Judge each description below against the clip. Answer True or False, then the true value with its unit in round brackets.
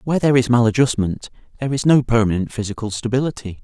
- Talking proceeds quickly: False (165 wpm)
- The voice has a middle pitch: False (120 Hz)